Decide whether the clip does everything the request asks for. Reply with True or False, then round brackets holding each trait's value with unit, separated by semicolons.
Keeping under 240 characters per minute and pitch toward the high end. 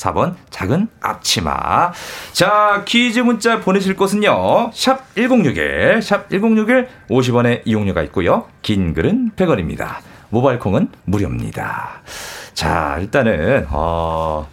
True (205 characters per minute; 200 Hz)